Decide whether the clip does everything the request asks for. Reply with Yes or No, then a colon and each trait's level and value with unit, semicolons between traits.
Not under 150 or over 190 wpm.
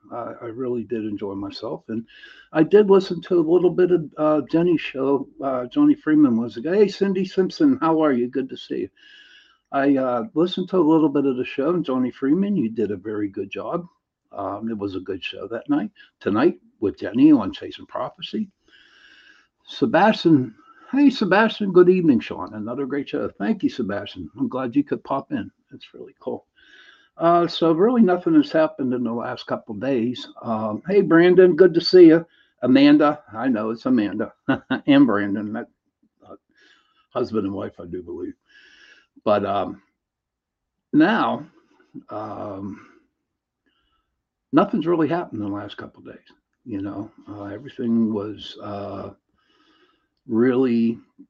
Yes: average, 165 wpm